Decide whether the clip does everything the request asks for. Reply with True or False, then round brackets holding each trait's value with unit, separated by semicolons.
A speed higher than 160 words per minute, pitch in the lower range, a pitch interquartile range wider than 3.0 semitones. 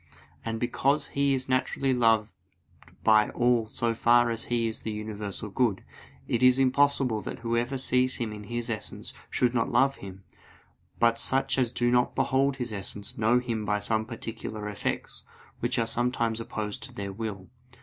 False (170 wpm; 115 Hz; 2.7 semitones)